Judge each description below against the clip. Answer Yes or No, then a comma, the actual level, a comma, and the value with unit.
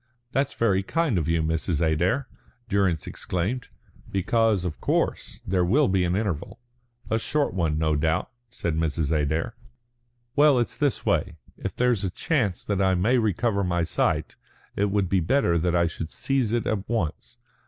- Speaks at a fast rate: No, average, 170 wpm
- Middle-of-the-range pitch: No, very low, 95 Hz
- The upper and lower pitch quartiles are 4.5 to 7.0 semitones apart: Yes, wide, 5.6 semitones